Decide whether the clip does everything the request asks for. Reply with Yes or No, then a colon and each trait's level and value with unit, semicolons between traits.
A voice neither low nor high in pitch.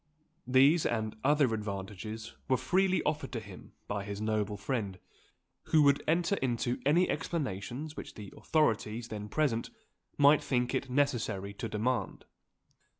No: low, 120 Hz